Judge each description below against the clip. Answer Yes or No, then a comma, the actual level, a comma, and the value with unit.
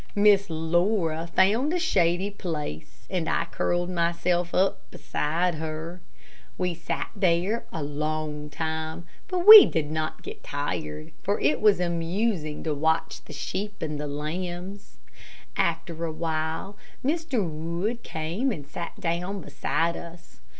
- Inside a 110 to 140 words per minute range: Yes, slow, 135 wpm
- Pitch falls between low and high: Yes, medium, 170 Hz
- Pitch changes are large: No, average, 3.5 semitones